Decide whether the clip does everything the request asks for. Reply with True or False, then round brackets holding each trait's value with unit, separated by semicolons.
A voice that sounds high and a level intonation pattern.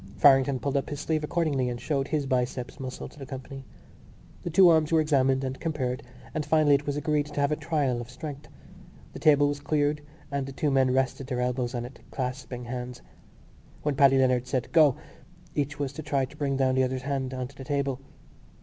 False (135 Hz; 2.2 semitones)